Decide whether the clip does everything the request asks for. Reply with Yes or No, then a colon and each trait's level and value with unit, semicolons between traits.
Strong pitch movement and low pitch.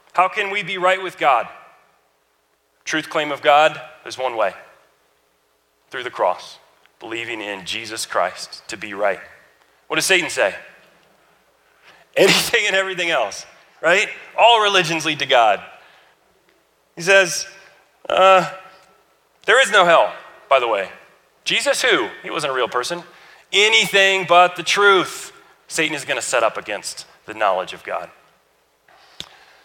No: wide, 7.2 semitones; medium, 175 Hz